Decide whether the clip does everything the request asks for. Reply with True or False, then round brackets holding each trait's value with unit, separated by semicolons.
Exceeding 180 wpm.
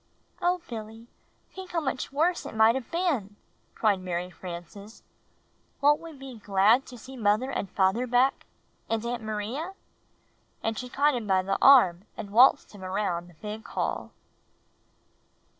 False (160 wpm)